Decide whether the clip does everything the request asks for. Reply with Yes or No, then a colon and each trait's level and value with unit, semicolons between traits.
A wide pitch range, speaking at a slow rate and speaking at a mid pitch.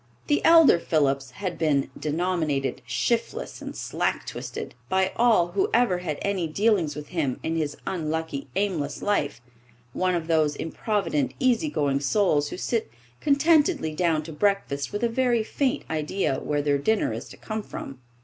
No: wide, 6.3 semitones; average, 160 wpm; medium, 170 Hz